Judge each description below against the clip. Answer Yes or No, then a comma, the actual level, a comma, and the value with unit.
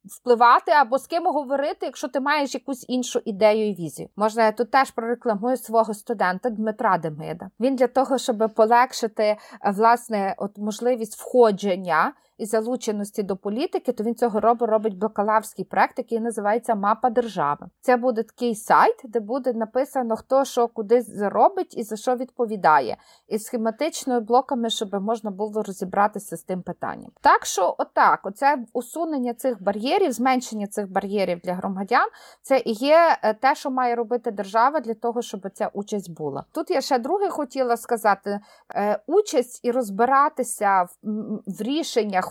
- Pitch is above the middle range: Yes, high, 230 Hz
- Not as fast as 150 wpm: No, fast, 155 wpm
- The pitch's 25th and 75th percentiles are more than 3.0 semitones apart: Yes, average, 3.4 semitones